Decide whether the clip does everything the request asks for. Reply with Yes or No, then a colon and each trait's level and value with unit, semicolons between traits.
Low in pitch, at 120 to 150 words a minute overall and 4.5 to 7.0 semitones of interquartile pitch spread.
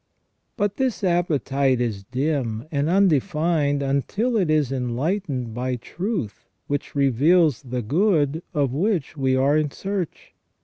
No: medium, 145 Hz; slow, 135 wpm; average, 5.2 semitones